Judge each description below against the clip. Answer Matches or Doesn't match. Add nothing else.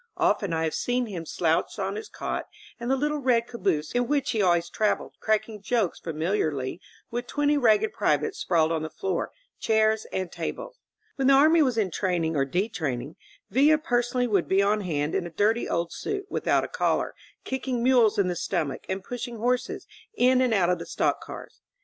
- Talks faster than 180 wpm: Matches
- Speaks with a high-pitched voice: Matches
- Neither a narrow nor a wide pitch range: Doesn't match